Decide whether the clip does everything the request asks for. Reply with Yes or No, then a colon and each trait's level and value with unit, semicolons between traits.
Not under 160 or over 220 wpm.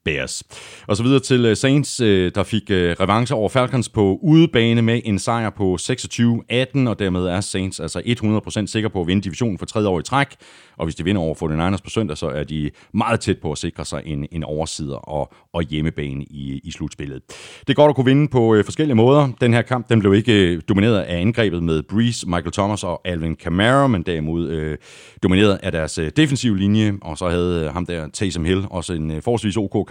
Yes: average, 210 wpm